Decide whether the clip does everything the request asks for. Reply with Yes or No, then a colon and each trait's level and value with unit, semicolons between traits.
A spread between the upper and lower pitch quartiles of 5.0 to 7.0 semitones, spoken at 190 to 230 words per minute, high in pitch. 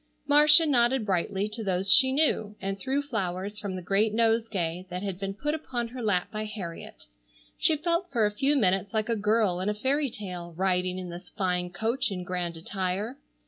No: average, 4.6 semitones; average, 195 wpm; high, 210 Hz